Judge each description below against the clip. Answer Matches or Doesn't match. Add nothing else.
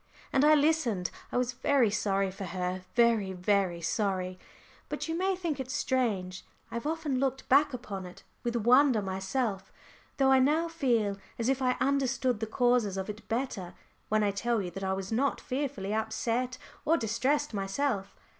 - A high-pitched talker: Matches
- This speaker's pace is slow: Doesn't match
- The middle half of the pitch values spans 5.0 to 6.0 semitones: Matches